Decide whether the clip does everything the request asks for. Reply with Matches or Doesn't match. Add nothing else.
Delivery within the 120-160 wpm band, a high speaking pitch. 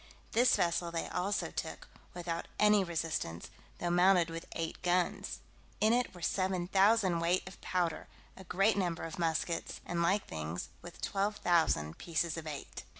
Doesn't match